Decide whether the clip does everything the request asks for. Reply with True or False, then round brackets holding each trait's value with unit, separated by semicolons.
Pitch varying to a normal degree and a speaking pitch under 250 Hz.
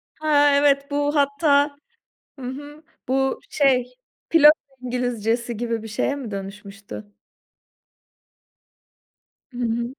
False (3.7 semitones; 255 Hz)